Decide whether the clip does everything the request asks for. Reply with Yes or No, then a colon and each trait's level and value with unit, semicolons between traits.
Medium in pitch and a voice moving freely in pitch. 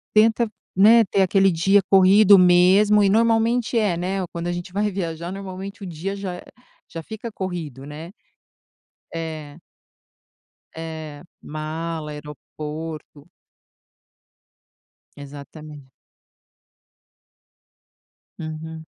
No: medium, 175 Hz; average, 4.0 semitones